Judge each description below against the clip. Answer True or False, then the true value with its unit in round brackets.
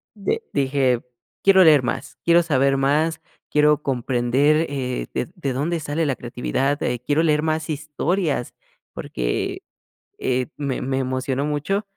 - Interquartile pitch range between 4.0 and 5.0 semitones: False (3.3 semitones)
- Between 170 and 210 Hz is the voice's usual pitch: False (145 Hz)